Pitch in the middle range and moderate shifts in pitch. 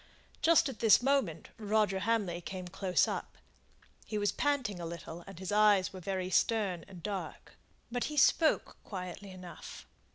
No: high, 195 Hz; average, 3.5 semitones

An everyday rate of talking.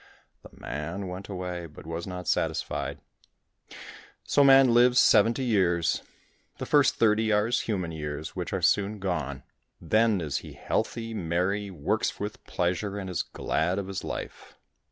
Yes: average, 155 wpm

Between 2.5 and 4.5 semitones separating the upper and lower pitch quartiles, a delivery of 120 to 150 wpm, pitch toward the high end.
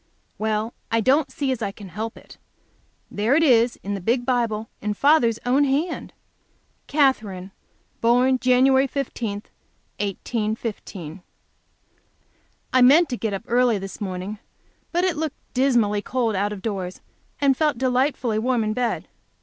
Yes: average, 4.0 semitones; average, 145 wpm; high, 235 Hz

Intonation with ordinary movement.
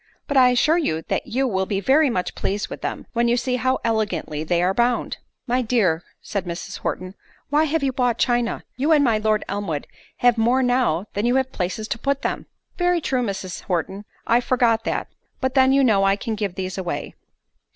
Yes: average, 4.9 semitones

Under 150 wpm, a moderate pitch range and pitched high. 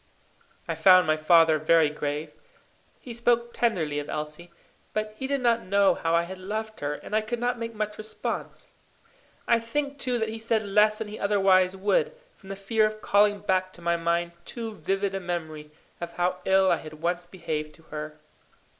No: average, 195 wpm; average, 4.5 semitones; high, 195 Hz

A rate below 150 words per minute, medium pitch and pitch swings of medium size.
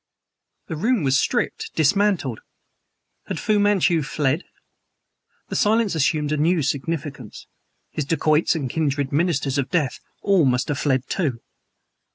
Yes: slow, 135 wpm; medium, 150 Hz; average, 4.3 semitones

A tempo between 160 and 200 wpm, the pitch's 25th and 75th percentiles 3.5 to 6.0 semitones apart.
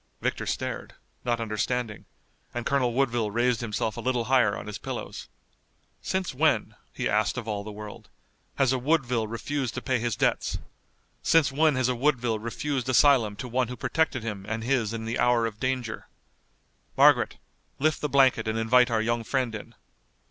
No: average, 175 wpm; average, 2.7 semitones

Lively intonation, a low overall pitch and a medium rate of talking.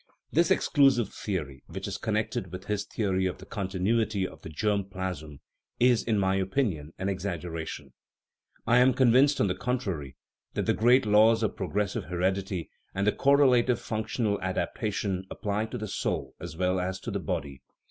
No: average, 3.6 semitones; low, 100 Hz; average, 170 wpm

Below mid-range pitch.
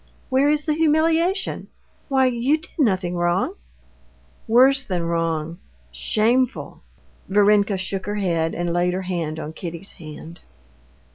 No: high, 190 Hz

